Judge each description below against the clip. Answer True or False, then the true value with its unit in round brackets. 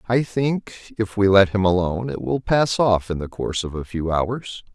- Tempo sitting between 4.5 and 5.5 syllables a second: True (5.0 syllables/s)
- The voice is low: True (105 Hz)